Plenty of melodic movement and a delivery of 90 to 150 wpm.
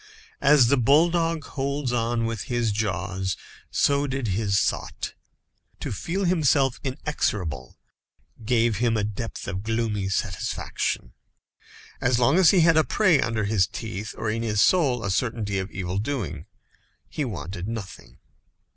Yes: wide, 5.7 semitones; average, 145 wpm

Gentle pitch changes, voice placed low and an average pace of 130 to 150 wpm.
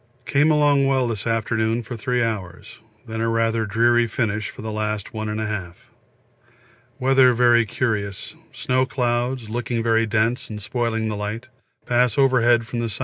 No: narrow, 2.2 semitones; low, 115 Hz; average, 160 wpm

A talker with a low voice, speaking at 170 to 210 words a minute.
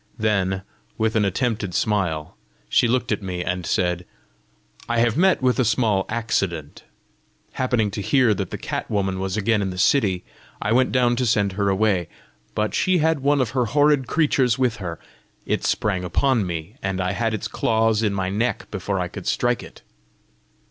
Yes: low, 110 Hz; average, 185 wpm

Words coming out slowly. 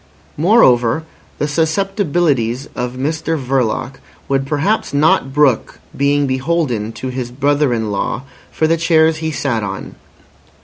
Yes: slow, 130 wpm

